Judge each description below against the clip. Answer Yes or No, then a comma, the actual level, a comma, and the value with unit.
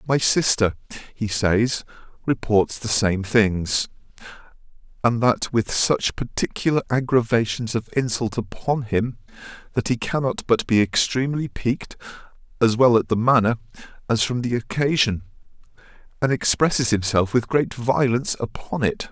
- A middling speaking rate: No, slow, 130 wpm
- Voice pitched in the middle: No, low, 115 Hz